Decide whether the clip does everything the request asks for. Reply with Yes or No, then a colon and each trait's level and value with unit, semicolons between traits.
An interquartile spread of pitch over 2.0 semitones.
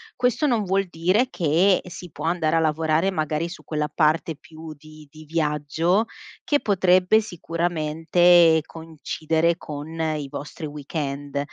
Yes: narrow, 2.6 semitones